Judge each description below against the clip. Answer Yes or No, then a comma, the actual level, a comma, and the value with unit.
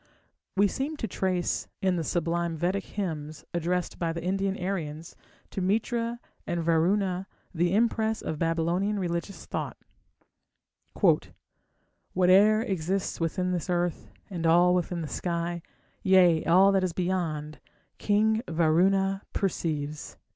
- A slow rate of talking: Yes, slow, 125 wpm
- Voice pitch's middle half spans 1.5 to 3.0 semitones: Yes, average, 2.7 semitones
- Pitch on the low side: No, medium, 180 Hz